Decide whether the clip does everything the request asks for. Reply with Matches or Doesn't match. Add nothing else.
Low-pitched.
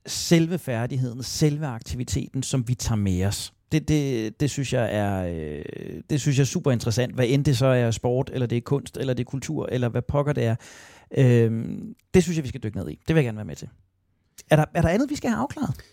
Matches